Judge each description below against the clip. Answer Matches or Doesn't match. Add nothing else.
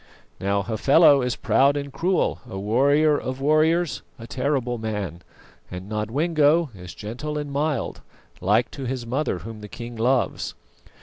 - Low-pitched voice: Matches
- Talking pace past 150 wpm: Doesn't match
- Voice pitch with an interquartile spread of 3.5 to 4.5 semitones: Doesn't match